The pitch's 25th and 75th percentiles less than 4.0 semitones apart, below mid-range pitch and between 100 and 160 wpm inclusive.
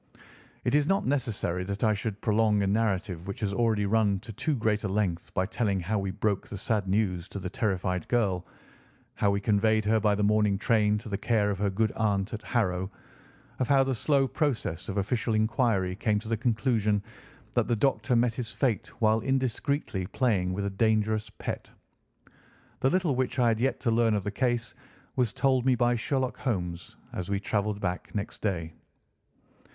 No: average, 3.1 semitones; low, 110 Hz; average, 195 wpm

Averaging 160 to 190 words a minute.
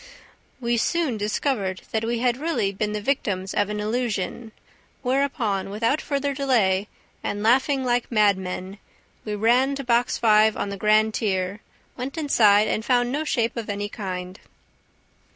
No: average, 150 wpm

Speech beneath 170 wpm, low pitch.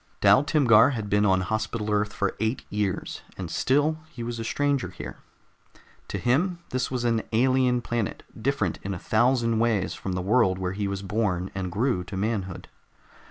No: average, 180 wpm; low, 110 Hz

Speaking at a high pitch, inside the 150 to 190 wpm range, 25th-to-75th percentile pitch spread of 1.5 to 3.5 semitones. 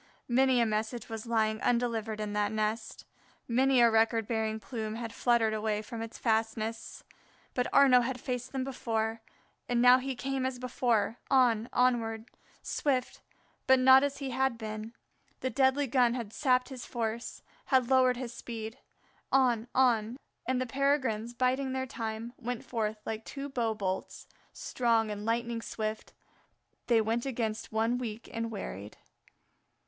Yes: high, 235 Hz; average, 155 wpm; narrow, 2.5 semitones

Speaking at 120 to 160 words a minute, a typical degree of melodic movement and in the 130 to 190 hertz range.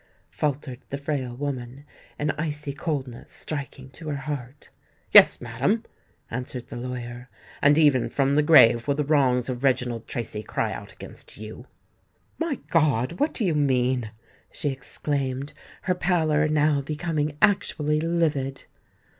Yes: average, 140 wpm; average, 3.3 semitones; medium, 140 Hz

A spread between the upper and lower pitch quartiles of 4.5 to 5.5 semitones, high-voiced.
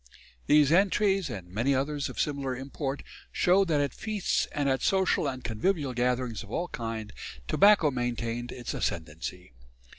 No: average, 5.1 semitones; low, 135 Hz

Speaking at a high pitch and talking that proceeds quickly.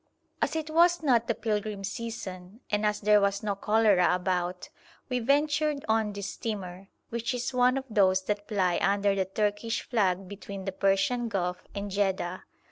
No: high, 205 Hz; average, 170 wpm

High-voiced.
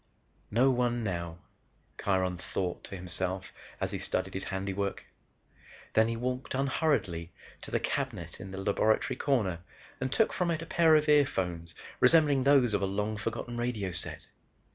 No: low, 110 Hz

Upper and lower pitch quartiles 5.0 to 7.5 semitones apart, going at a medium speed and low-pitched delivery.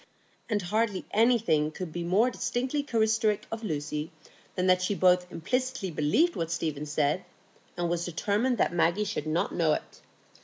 No: average, 5.3 semitones; average, 160 wpm; medium, 185 Hz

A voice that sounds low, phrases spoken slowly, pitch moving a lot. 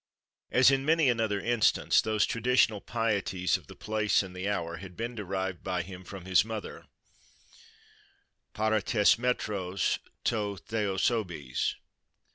No: low, 105 Hz; slow, 125 wpm; average, 3.3 semitones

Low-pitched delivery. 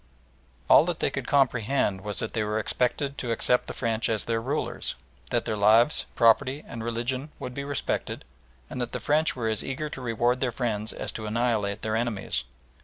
Yes: low, 120 Hz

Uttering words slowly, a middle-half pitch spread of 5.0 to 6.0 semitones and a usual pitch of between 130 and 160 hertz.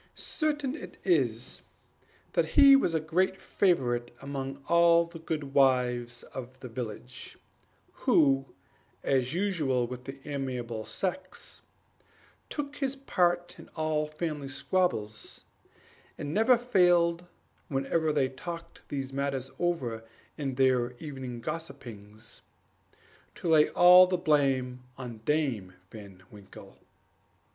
Yes: slow, 115 wpm; wide, 5.4 semitones; medium, 140 Hz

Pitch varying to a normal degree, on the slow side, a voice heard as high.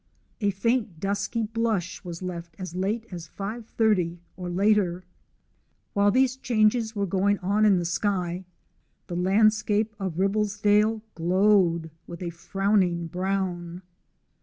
Yes: average, 3.2 semitones; slow, 125 wpm; high, 195 Hz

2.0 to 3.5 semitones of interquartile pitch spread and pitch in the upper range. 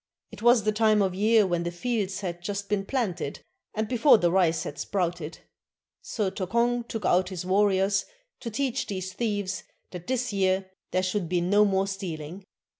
Yes: average, 2.9 semitones; high, 195 Hz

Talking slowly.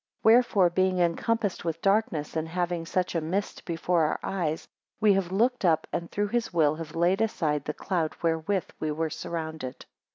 No: average, 185 wpm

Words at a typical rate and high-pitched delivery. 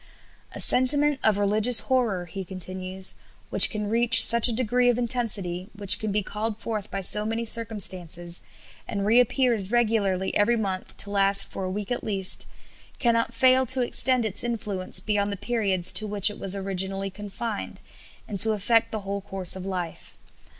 Yes: average, 170 wpm; high, 205 Hz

